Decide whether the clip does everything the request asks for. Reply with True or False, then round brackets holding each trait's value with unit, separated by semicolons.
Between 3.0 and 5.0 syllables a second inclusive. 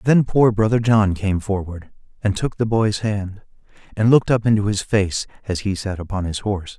False (5.2 syllables/s)